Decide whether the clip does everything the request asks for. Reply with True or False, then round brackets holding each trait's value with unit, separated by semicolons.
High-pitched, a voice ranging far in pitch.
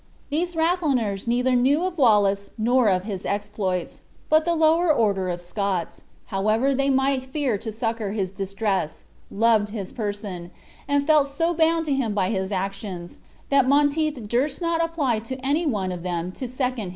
True (235 Hz; 6.3 semitones)